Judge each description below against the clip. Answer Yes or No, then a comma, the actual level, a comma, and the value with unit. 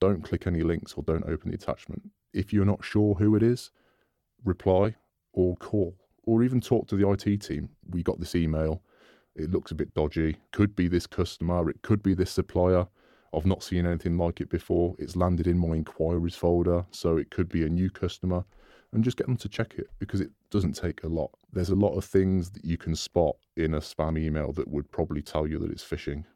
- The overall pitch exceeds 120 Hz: No, very low, 90 Hz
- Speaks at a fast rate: Yes, fast, 225 wpm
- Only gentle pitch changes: No, average, 3.4 semitones